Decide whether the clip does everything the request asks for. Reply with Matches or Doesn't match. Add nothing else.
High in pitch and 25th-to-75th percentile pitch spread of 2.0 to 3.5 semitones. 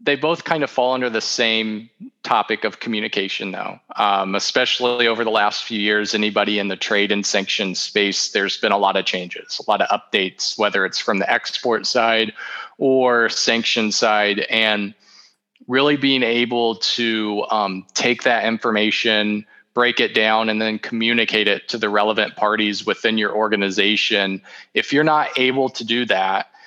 Doesn't match